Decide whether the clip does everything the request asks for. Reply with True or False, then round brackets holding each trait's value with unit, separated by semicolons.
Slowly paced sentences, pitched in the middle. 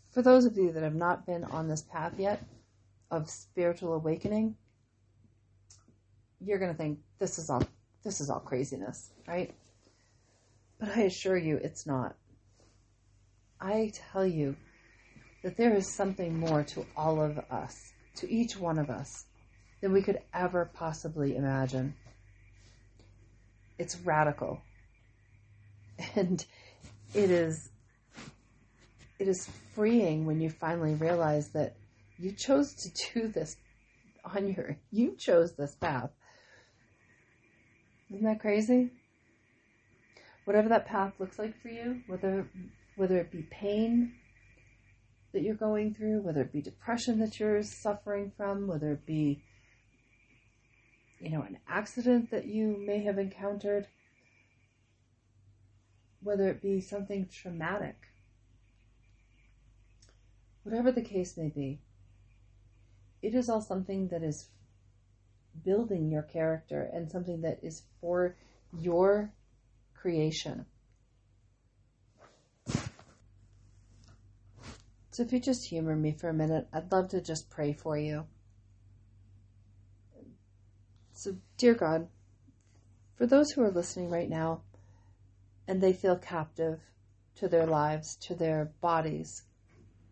True (120 wpm; 150 Hz)